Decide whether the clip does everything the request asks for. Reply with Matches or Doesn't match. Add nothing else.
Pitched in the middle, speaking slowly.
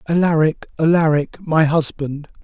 Matches